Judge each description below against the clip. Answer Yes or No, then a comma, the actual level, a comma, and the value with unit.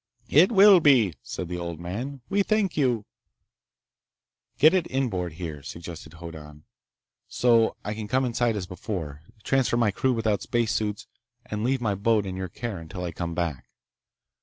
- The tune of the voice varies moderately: No, wide, 6.4 semitones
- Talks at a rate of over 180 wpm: No, average, 160 wpm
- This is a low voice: Yes, low, 105 Hz